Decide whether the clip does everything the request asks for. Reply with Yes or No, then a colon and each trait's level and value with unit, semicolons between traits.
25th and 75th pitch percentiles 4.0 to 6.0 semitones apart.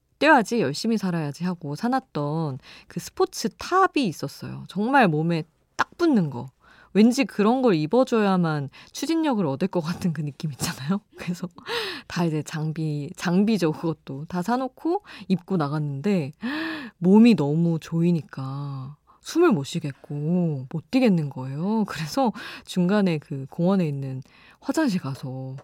No: wide, 7.5 semitones